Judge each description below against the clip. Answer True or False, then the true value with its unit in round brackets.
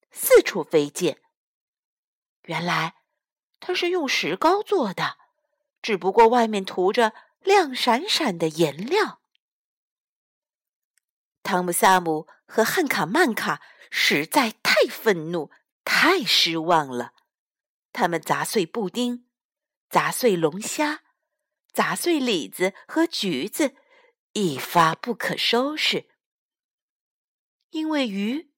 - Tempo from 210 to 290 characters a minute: False (145 characters per minute)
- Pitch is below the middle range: False (245 Hz)